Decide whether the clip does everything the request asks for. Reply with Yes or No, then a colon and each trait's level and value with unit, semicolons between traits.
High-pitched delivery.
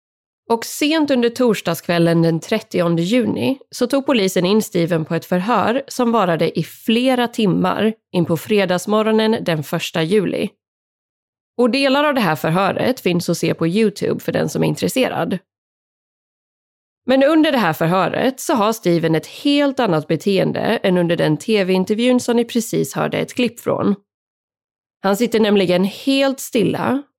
Yes: high, 205 Hz